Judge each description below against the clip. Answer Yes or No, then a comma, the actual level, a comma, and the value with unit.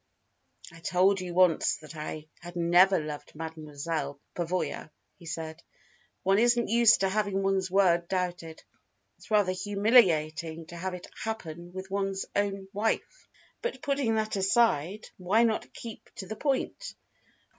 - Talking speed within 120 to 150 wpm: Yes, average, 145 wpm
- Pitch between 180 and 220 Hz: Yes, medium, 185 Hz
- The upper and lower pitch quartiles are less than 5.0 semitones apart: Yes, average, 3.8 semitones